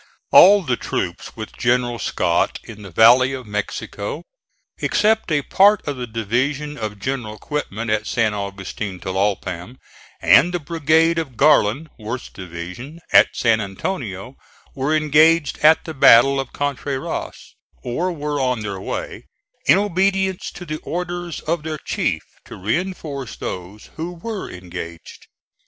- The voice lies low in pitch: Yes, low, 130 Hz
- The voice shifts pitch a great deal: Yes, wide, 7.0 semitones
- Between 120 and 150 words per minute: Yes, average, 140 wpm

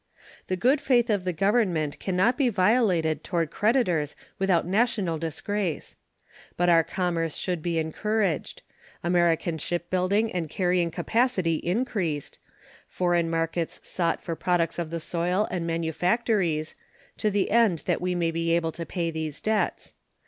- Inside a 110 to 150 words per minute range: Yes, average, 145 wpm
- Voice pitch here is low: No, medium, 175 Hz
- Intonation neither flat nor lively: Yes, average, 3.6 semitones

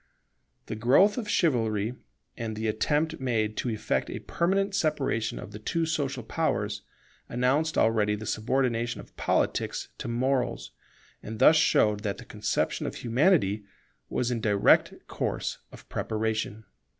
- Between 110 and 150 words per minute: Yes, average, 140 wpm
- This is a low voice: Yes, low, 120 Hz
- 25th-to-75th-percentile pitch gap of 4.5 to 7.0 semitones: Yes, average, 5.3 semitones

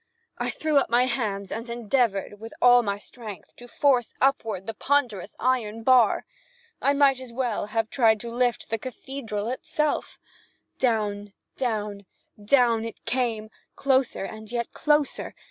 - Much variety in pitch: No, average, 3.2 semitones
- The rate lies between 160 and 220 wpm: No, average, 145 wpm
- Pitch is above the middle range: Yes, high, 235 Hz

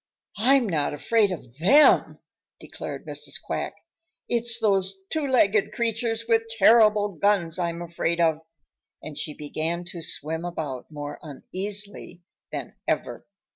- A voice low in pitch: No, high, 190 Hz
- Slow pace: Yes, slow, 130 wpm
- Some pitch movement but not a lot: No, wide, 5.8 semitones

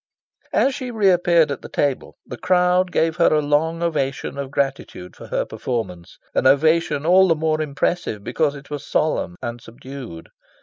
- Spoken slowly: No, average, 175 wpm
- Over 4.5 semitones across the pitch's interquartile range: No, average, 4.0 semitones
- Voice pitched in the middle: Yes, medium, 150 Hz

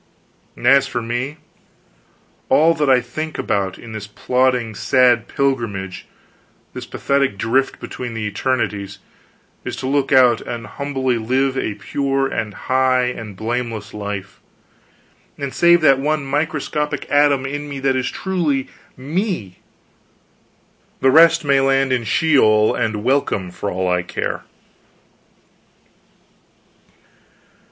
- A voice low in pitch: Yes, low, 130 Hz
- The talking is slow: Yes, slow, 125 wpm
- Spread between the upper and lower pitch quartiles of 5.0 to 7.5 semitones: No, average, 4.0 semitones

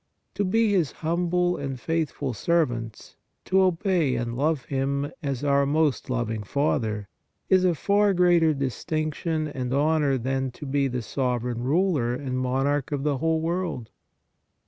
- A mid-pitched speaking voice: Yes, medium, 145 Hz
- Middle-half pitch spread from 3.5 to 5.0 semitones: Yes, average, 4.6 semitones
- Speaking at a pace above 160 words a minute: No, average, 145 wpm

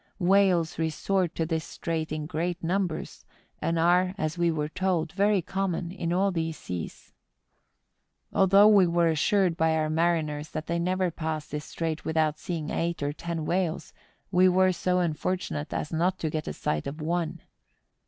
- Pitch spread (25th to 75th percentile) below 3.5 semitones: Yes, narrow, 2.6 semitones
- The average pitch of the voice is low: No, medium, 170 Hz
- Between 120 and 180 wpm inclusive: Yes, average, 170 wpm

